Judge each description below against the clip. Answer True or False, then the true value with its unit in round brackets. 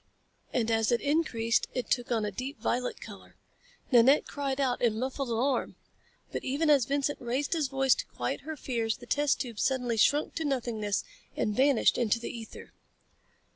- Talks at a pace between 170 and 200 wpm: True (175 wpm)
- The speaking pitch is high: True (255 Hz)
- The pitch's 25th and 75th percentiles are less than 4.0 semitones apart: True (3.4 semitones)